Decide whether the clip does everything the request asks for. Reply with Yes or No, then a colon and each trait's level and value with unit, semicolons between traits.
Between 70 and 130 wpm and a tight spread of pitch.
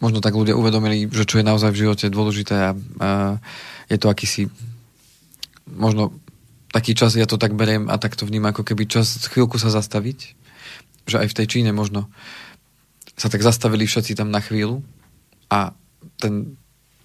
No: fast, 165 wpm; narrow, 1.9 semitones